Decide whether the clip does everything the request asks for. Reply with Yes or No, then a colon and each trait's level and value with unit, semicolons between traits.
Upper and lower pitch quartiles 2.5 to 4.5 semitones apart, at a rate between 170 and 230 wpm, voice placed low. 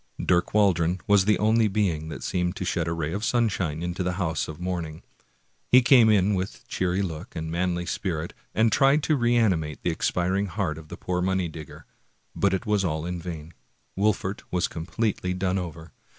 Yes: average, 3.6 semitones; average, 190 wpm; very low, 90 Hz